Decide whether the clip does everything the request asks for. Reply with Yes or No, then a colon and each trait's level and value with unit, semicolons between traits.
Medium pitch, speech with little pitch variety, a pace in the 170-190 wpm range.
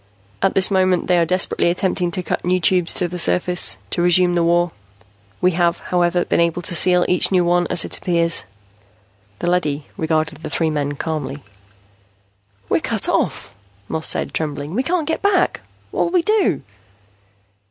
Yes: medium, 175 Hz; narrow, 1.8 semitones; average, 175 wpm